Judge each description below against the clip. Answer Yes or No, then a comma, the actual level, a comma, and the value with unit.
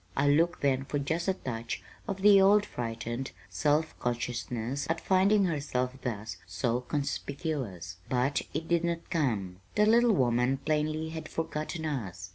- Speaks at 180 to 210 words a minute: No, average, 150 wpm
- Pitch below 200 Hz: Yes, medium, 140 Hz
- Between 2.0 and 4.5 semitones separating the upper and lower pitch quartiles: No, average, 5.2 semitones